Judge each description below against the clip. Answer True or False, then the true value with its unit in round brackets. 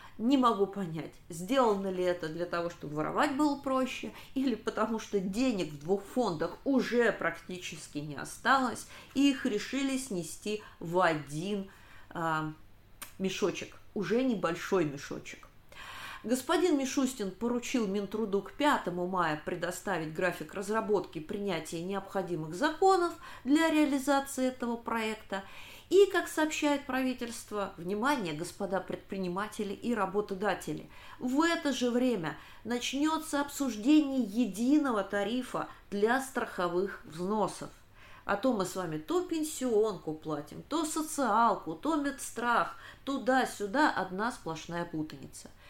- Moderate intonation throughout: False (6.7 semitones)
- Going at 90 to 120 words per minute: True (115 wpm)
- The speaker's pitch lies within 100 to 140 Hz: False (210 Hz)